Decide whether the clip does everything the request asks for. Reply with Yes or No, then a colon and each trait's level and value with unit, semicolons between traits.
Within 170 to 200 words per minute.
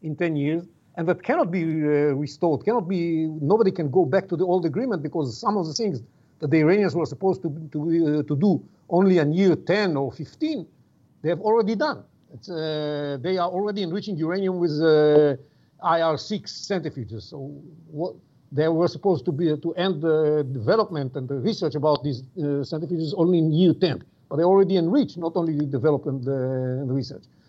Yes: average, 195 wpm